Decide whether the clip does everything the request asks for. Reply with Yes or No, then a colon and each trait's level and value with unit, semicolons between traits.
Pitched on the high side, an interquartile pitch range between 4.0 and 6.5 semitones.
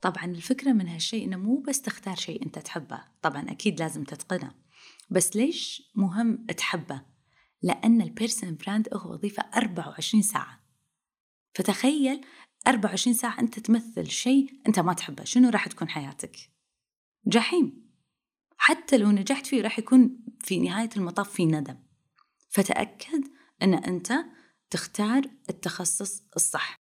Yes: high, 215 Hz; wide, 5.6 semitones